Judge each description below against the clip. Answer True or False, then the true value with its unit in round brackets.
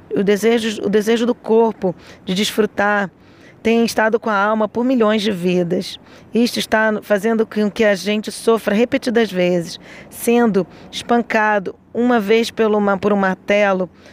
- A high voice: True (215 Hz)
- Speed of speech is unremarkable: True (145 wpm)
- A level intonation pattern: True (2.2 semitones)